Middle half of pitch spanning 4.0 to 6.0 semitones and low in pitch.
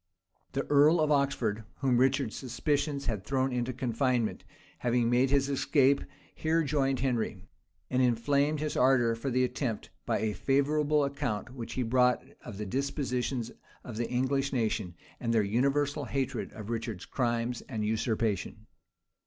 No: average, 3.2 semitones; low, 125 Hz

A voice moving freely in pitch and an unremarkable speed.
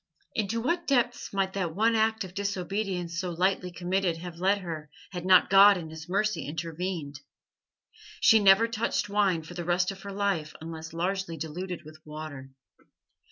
No: average, 3.4 semitones; average, 165 wpm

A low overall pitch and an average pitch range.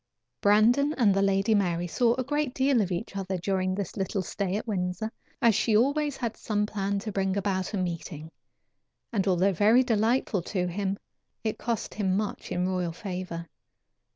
No: high, 200 Hz; average, 3.2 semitones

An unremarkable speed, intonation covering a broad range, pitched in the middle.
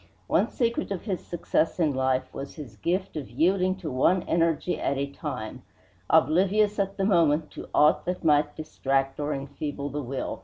No: average, 180 wpm; average, 4.7 semitones; medium, 155 Hz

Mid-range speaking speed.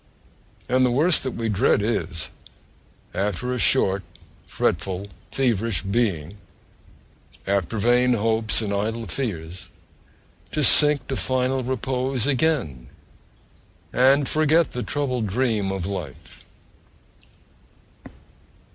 No: slow, 100 wpm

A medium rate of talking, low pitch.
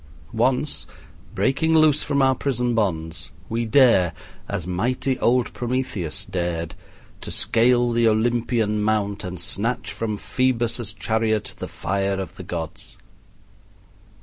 No: slow, 120 wpm; low, 115 Hz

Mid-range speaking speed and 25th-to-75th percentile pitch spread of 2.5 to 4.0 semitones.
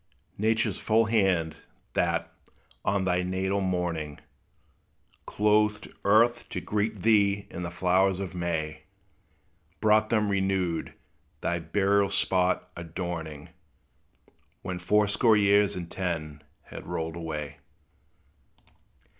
No: slow, 105 wpm; average, 3.2 semitones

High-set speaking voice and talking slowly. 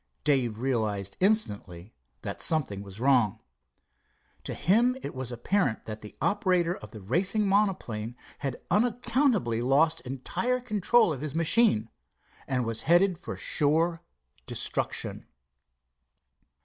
No: medium, 145 Hz; slow, 120 wpm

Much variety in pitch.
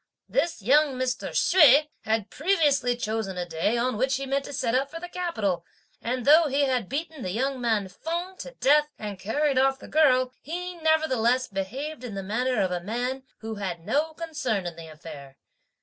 Yes: wide, 6.1 semitones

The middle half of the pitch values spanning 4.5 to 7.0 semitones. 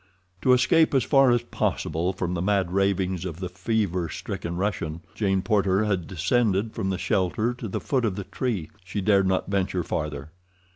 No: average, 3.1 semitones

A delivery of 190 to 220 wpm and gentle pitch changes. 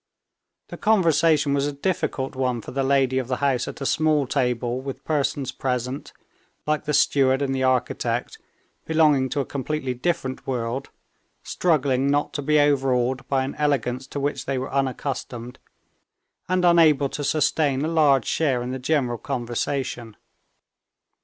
No: average, 155 wpm; narrow, 2.3 semitones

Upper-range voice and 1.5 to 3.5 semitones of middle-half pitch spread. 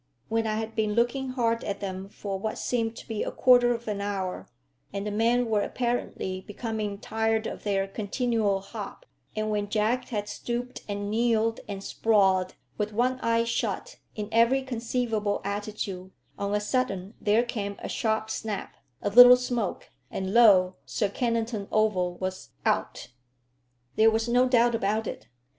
Yes: high, 220 Hz; average, 2.7 semitones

